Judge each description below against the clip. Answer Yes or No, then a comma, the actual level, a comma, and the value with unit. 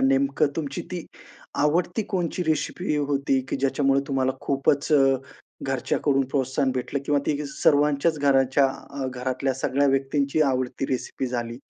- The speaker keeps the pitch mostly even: Yes, narrow, 1.5 semitones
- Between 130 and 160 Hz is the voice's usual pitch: Yes, medium, 140 Hz